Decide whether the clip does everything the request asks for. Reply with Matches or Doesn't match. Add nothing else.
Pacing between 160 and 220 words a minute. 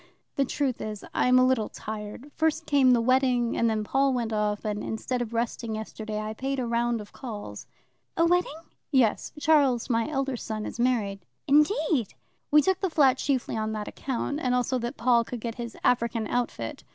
Matches